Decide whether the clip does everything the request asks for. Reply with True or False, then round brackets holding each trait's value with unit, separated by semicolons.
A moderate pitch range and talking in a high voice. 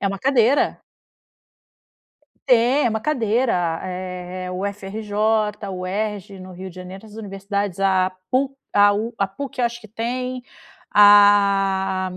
True (3.1 semitones; 205 Hz)